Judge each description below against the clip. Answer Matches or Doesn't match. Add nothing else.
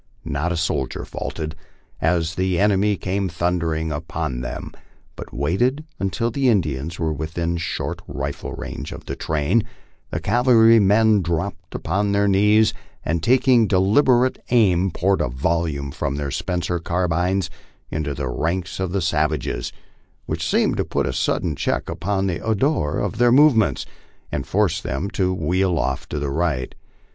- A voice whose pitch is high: Doesn't match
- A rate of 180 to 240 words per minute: Doesn't match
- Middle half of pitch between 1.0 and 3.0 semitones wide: Doesn't match